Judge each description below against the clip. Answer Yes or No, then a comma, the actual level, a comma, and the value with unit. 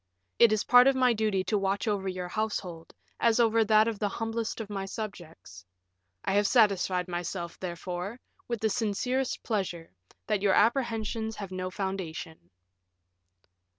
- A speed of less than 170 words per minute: Yes, average, 150 wpm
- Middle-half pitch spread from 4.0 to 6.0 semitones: No, average, 3.3 semitones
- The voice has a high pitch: Yes, high, 205 Hz